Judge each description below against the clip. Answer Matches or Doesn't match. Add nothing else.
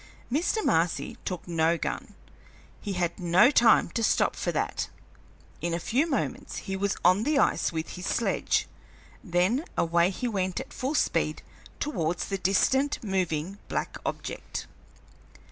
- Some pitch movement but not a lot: Doesn't match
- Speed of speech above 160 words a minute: Doesn't match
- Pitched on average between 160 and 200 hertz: Matches